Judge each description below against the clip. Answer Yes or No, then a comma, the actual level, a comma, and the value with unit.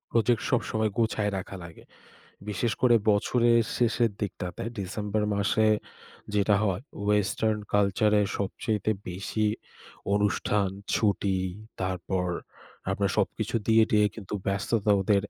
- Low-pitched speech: Yes, low, 105 Hz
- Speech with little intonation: Yes, narrow, 2.0 semitones